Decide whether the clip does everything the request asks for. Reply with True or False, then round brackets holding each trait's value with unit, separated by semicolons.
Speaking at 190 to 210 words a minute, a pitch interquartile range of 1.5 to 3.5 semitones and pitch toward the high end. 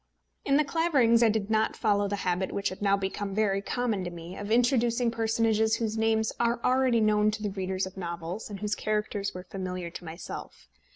True (205 wpm; 3.0 semitones; 210 Hz)